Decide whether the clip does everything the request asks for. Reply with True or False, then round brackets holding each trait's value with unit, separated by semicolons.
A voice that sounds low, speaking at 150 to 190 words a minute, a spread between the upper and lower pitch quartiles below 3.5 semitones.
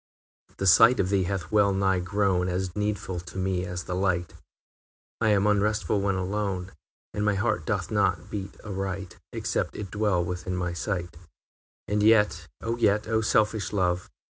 True (95 Hz; 175 wpm; 2.5 semitones)